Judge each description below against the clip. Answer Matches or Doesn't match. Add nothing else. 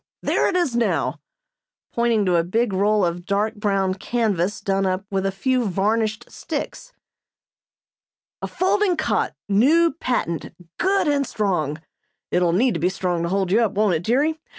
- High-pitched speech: Matches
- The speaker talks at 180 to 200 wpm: Doesn't match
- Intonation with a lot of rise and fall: Doesn't match